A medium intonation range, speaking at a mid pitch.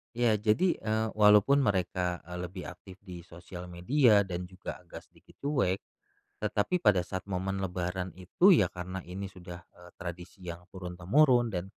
No: average, 3.1 semitones; very low, 95 Hz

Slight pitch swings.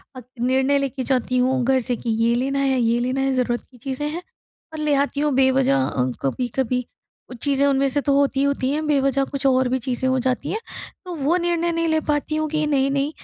Yes: narrow, 2.1 semitones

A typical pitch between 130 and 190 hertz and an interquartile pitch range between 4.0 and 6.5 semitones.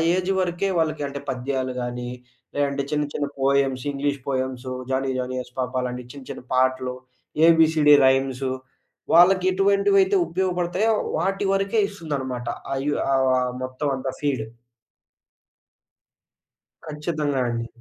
Yes: medium, 140 Hz; average, 4.6 semitones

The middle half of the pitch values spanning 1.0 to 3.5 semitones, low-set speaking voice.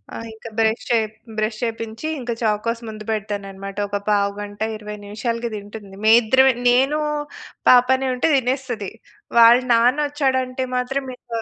No: average, 3.1 semitones; high, 230 Hz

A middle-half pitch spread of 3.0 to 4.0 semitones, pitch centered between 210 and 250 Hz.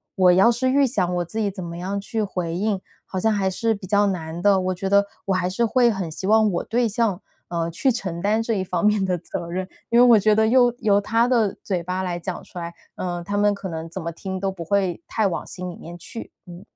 No: average, 3.4 semitones; high, 190 Hz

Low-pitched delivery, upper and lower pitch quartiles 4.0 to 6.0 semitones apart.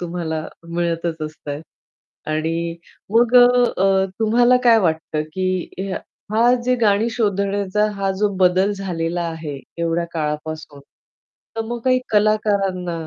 No: medium, 185 Hz; average, 4.5 semitones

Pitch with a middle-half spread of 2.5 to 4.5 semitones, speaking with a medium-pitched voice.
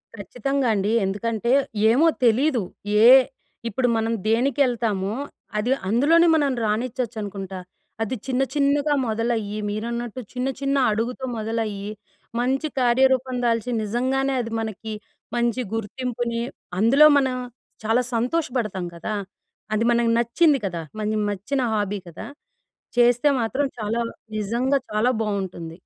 No: average, 3.4 semitones; high, 235 Hz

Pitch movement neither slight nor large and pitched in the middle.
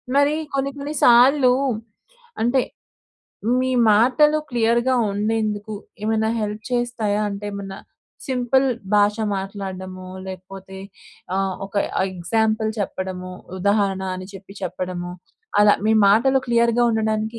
No: average, 3.8 semitones; high, 215 Hz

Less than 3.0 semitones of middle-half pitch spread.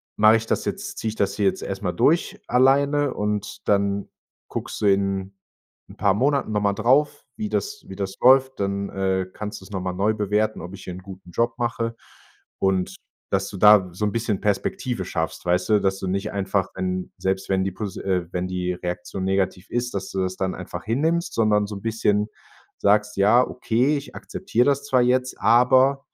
No: average, 4.0 semitones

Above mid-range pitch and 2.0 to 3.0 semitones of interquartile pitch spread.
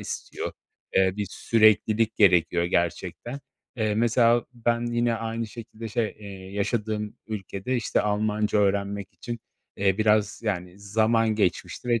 No: low, 110 Hz; narrow, 2.4 semitones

